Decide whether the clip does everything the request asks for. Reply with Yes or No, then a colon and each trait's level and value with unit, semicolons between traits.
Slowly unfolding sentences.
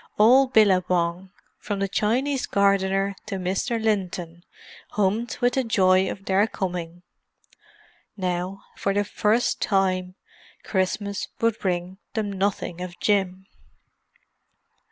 Yes: slow, 115 wpm